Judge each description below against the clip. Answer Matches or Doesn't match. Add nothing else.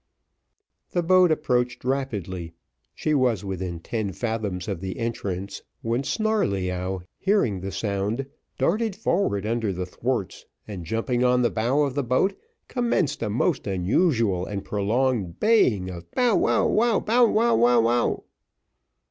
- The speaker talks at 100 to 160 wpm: Matches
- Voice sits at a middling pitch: Doesn't match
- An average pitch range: Doesn't match